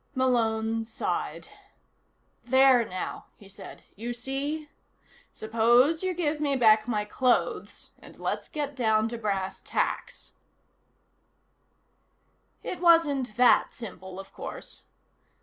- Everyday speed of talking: No, slow, 110 wpm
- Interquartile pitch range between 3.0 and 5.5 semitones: Yes, average, 4.2 semitones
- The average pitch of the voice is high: Yes, high, 240 Hz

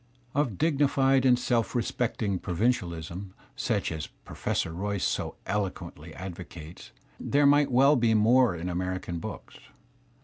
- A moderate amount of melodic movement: No, wide, 6.4 semitones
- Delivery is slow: Yes, slow, 130 wpm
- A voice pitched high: No, low, 105 Hz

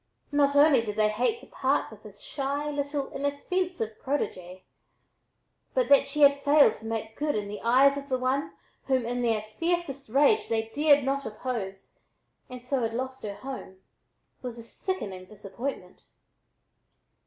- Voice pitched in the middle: No, very high, 260 Hz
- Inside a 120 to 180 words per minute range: Yes, average, 160 wpm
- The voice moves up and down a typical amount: Yes, average, 4.4 semitones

